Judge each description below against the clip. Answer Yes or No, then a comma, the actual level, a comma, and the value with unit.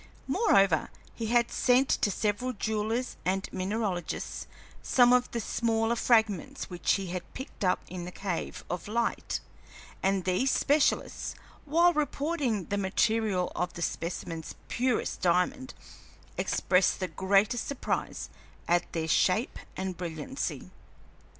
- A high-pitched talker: Yes, high, 205 Hz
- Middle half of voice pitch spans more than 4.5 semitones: Yes, average, 5.1 semitones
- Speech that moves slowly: Yes, slow, 125 wpm